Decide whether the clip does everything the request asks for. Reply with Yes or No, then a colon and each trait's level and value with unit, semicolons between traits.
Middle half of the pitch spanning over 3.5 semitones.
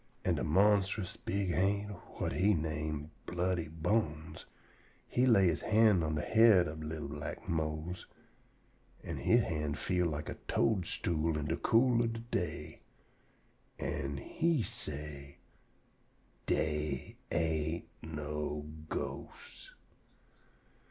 Yes: average, 4.8 semitones